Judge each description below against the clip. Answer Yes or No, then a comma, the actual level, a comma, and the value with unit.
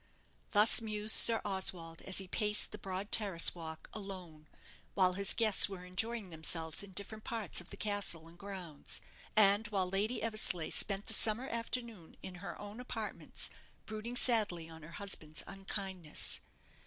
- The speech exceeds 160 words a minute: No, average, 155 wpm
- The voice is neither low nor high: No, high, 195 Hz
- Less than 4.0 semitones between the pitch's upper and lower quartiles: Yes, average, 3.4 semitones